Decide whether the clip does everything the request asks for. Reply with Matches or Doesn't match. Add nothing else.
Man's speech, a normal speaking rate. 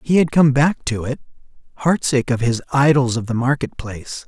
Matches